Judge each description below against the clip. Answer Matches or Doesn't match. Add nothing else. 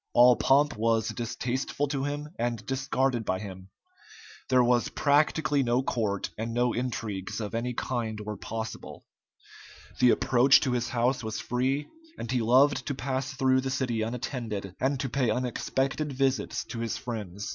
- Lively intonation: Doesn't match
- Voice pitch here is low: Matches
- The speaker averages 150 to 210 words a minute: Matches